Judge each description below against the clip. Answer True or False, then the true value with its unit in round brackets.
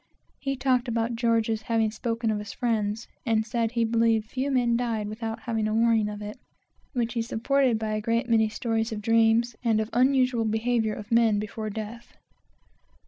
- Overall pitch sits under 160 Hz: False (225 Hz)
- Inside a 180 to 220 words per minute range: True (185 wpm)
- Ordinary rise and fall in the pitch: False (1.5 semitones)